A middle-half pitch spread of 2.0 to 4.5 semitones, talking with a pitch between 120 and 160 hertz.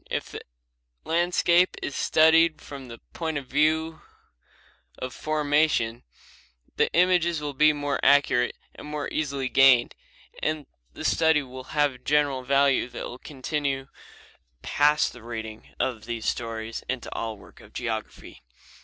Yes: average, 3.6 semitones; medium, 140 Hz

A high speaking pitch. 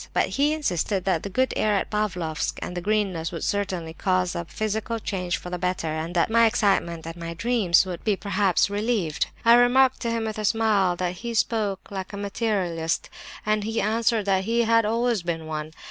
Yes: high, 200 Hz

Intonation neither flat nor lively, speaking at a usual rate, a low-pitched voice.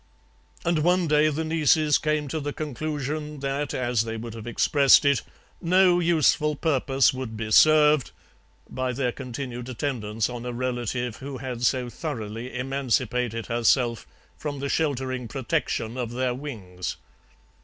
Yes: average, 3.8 semitones; average, 145 wpm; low, 130 Hz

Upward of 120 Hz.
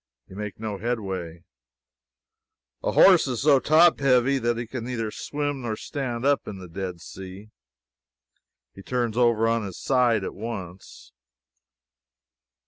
No: low, 115 Hz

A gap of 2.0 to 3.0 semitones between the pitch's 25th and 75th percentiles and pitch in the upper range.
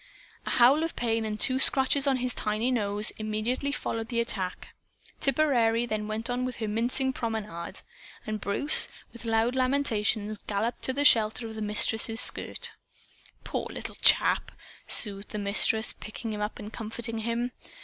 Yes: average, 2.7 semitones; high, 225 Hz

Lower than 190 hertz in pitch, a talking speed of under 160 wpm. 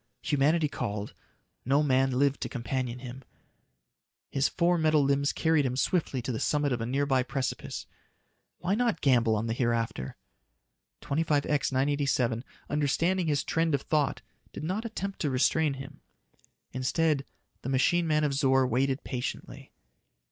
Yes: medium, 140 Hz; average, 145 wpm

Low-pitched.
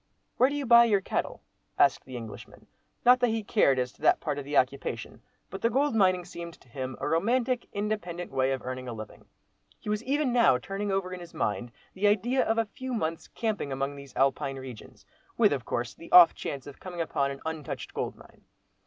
No: medium, 175 Hz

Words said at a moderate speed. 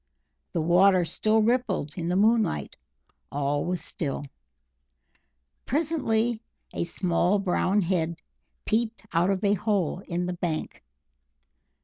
No: slow, 115 wpm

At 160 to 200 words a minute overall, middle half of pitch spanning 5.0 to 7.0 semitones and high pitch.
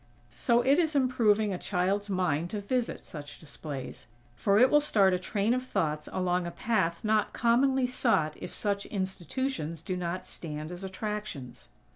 Yes: average, 165 wpm; wide, 5.4 semitones; high, 200 Hz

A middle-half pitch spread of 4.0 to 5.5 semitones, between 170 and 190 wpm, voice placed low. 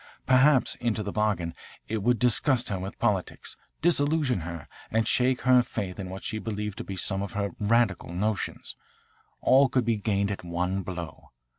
Yes: average, 4.3 semitones; average, 175 wpm; low, 105 Hz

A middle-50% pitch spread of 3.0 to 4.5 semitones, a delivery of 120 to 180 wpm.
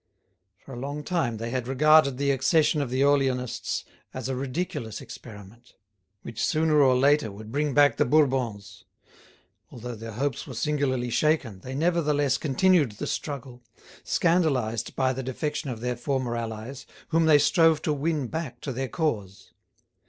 Yes: average, 3.7 semitones; average, 160 wpm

